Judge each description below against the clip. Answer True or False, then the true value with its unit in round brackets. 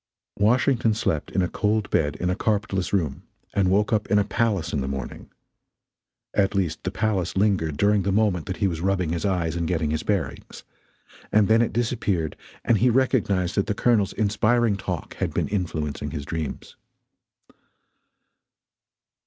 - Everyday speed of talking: True (170 wpm)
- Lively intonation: False (4.0 semitones)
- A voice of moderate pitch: False (100 Hz)